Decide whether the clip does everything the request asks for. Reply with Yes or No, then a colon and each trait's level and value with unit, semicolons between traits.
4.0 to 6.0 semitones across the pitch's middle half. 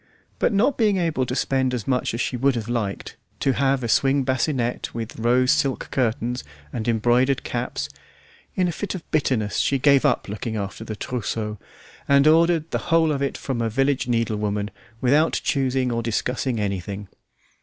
No: average, 3.5 semitones